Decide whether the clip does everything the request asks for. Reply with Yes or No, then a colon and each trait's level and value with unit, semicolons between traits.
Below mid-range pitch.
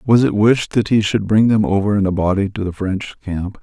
Yes: low, 105 Hz